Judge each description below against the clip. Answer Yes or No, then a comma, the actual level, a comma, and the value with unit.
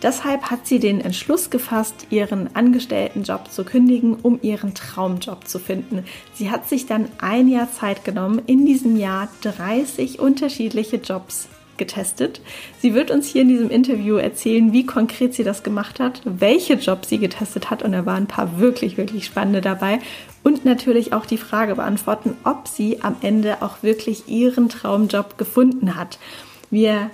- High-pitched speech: Yes, high, 225 Hz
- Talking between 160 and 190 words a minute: Yes, average, 170 wpm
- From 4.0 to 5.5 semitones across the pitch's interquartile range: No, average, 3.5 semitones